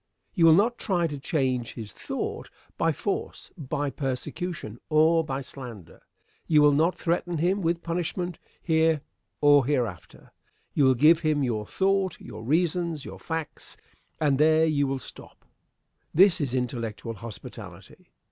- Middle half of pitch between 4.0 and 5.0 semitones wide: Yes, average, 4.3 semitones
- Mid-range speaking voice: Yes, medium, 155 Hz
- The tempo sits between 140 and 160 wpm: Yes, average, 145 wpm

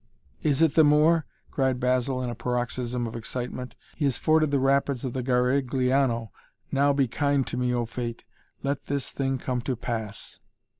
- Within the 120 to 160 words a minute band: No, average, 180 wpm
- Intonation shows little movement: Yes, narrow, 2.3 semitones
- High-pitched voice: No, low, 130 Hz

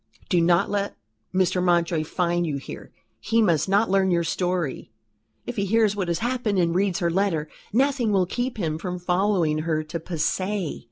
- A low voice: No, medium, 180 Hz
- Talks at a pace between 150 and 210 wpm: Yes, average, 180 wpm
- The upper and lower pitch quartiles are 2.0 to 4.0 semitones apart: Yes, average, 3.2 semitones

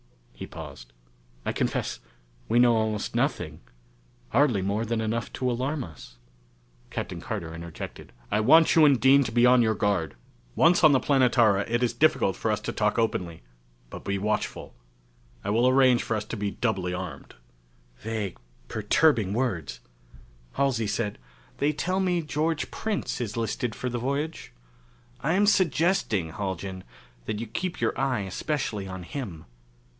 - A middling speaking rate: Yes, average, 160 wpm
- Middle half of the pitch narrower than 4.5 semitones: No, wide, 5.5 semitones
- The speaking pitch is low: Yes, low, 115 Hz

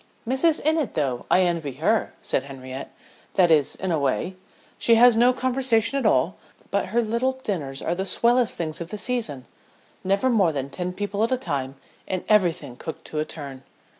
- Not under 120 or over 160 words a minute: No, average, 190 wpm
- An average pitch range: No, wide, 8.0 semitones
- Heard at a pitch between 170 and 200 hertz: Yes, high, 190 Hz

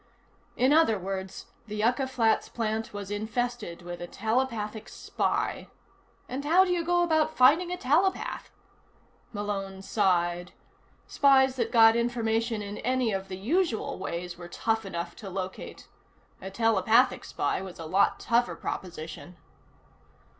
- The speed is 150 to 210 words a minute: No, average, 140 wpm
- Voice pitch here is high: Yes, high, 220 Hz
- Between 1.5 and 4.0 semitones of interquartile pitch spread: No, average, 4.9 semitones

